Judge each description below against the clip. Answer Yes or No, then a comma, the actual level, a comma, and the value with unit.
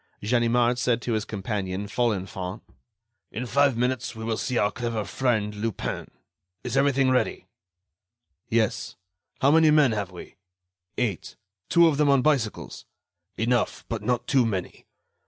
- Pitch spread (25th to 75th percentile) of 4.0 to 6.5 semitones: No, average, 3.6 semitones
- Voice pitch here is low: Yes, low, 120 Hz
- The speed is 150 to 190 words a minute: No, slow, 135 wpm